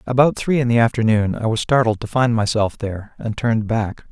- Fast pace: Yes, fast, 220 wpm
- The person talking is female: No, male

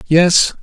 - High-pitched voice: No, medium, 170 Hz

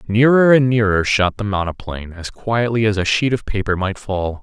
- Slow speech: No, fast, 205 wpm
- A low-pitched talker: Yes, low, 105 Hz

